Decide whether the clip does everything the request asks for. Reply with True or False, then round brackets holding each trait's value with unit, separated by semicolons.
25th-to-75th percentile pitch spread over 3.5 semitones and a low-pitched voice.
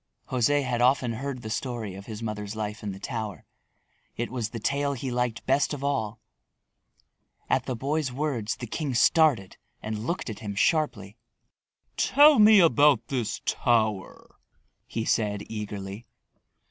True (4.5 semitones; 120 Hz)